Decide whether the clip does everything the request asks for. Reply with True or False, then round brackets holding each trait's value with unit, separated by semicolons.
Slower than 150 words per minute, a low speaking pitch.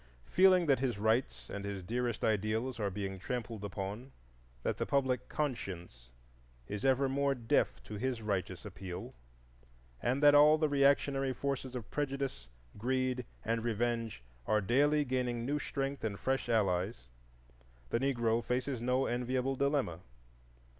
True (140 wpm; 125 Hz)